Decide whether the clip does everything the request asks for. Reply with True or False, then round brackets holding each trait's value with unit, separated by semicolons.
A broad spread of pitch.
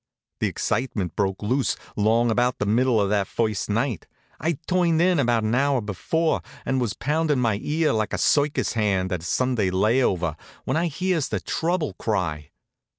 True (6.1 semitones)